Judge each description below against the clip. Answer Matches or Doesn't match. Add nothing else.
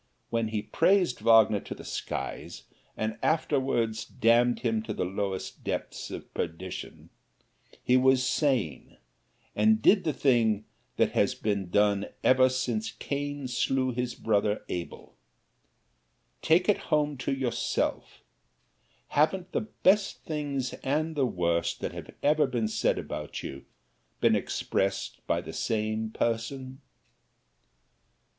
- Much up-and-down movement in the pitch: Doesn't match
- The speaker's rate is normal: Doesn't match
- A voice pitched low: Matches